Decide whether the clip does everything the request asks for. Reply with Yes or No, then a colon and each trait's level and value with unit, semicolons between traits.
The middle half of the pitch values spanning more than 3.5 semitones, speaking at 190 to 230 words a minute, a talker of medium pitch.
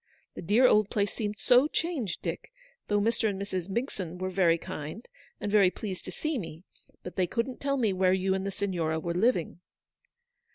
No: average, 3.9 semitones; average, 195 wpm; high, 200 Hz